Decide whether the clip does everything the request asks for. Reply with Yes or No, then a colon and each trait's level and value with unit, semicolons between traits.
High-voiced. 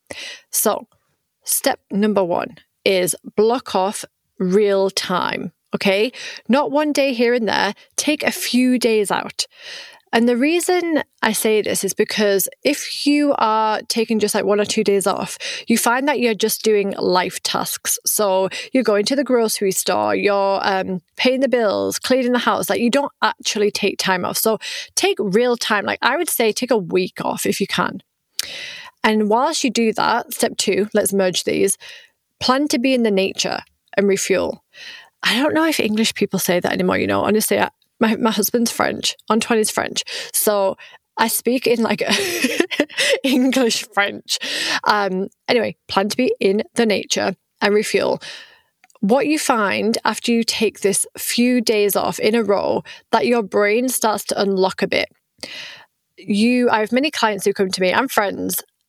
Yes: high, 225 Hz